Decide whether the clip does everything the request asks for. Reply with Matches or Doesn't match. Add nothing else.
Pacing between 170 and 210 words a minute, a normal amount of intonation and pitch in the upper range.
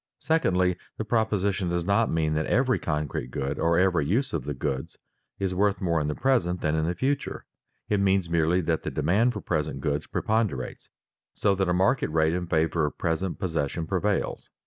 Doesn't match